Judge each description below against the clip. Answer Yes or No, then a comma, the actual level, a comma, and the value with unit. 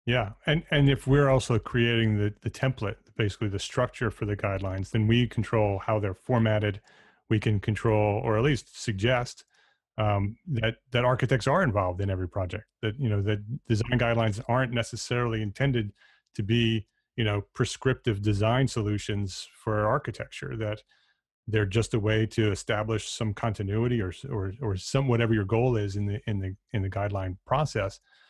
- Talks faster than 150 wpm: Yes, average, 170 wpm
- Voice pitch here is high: No, low, 110 Hz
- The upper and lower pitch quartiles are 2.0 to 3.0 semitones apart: Yes, narrow, 2.6 semitones